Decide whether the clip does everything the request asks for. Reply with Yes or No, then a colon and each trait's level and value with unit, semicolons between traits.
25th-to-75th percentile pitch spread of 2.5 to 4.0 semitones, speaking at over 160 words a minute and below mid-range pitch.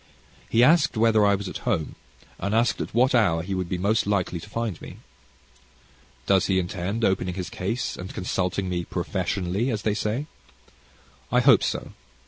Yes: average, 3.7 semitones; average, 175 wpm; low, 100 Hz